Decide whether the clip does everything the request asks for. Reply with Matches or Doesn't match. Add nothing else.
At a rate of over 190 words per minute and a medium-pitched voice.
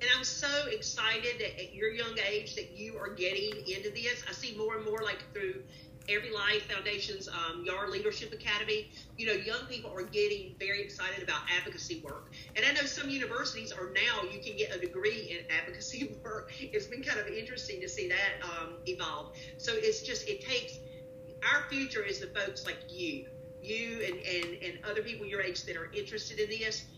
Doesn't match